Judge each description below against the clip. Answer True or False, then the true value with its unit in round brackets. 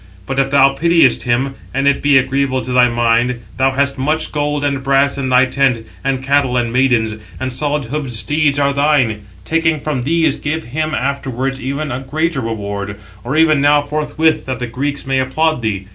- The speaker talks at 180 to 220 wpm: True (190 wpm)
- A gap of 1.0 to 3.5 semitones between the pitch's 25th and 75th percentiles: True (2.6 semitones)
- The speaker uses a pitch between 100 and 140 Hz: True (135 Hz)